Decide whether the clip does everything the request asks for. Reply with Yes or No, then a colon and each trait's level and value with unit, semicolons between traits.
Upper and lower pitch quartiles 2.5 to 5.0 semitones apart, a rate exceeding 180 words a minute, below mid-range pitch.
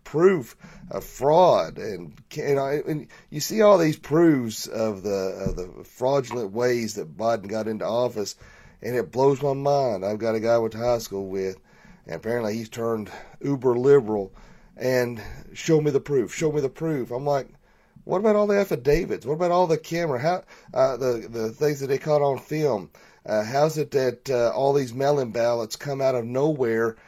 Yes: average, 4.7 semitones; average, 195 wpm; low, 130 Hz